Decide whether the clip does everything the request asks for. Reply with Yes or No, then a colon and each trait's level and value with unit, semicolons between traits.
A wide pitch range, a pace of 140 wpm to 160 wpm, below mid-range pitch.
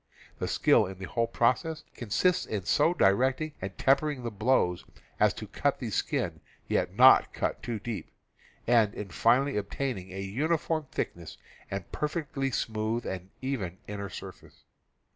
Yes: wide, 5.8 semitones; average, 150 wpm; low, 115 Hz